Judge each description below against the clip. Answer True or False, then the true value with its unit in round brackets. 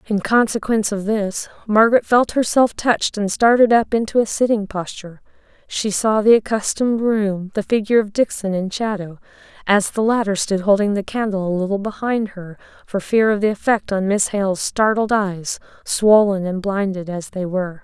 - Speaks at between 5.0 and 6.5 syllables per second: True (5.2 syllables/s)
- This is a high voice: True (205 Hz)